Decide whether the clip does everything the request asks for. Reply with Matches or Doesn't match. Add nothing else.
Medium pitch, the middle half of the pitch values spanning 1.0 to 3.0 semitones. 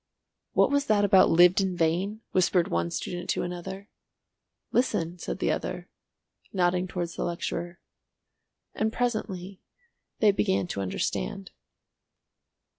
Matches